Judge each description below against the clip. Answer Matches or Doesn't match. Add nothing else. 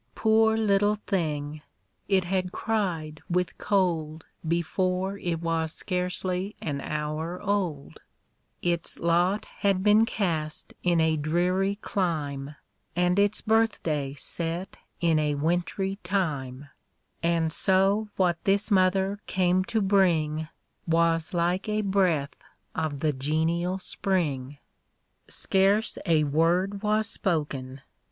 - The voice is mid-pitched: Matches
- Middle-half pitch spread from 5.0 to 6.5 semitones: Doesn't match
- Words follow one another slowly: Matches